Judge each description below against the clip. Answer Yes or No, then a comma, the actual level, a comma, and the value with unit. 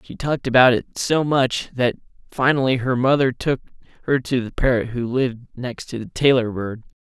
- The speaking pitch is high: No, low, 125 Hz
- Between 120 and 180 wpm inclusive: No, average, 190 wpm